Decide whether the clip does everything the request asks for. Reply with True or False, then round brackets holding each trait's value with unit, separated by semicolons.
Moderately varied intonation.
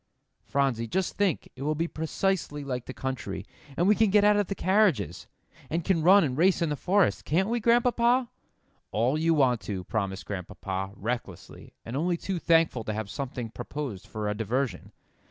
False (8.8 semitones)